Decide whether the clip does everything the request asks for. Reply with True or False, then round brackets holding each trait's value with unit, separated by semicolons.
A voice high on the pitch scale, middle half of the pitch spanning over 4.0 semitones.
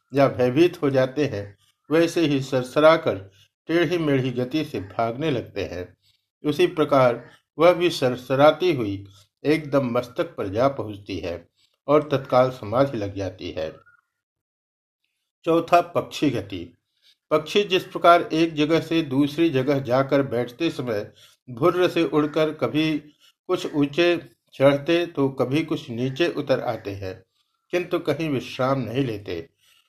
False (140 Hz; 5.0 semitones)